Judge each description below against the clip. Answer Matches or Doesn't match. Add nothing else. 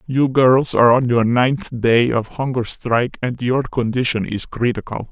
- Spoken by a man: Doesn't match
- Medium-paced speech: Matches